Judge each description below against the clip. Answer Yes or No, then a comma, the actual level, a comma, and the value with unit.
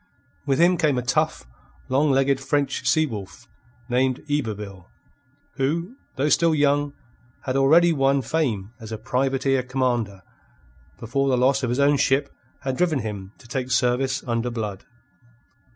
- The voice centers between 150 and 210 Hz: No, low, 135 Hz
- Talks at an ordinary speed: Yes, average, 150 wpm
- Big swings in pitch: No, average, 2.8 semitones